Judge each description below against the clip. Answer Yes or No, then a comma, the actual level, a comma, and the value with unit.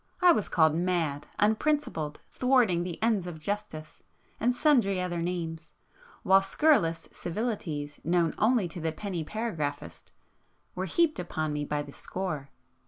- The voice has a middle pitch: Yes, medium, 175 Hz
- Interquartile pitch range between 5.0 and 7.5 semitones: Yes, wide, 5.4 semitones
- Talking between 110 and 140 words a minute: Yes, slow, 135 wpm